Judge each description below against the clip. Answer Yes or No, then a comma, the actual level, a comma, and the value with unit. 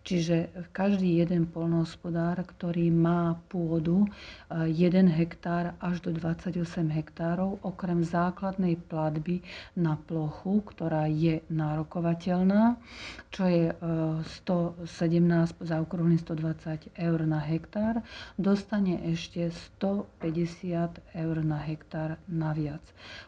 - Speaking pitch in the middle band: Yes, medium, 170 Hz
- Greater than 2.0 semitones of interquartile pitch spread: No, narrow, 1.7 semitones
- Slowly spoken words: Yes, slow, 95 wpm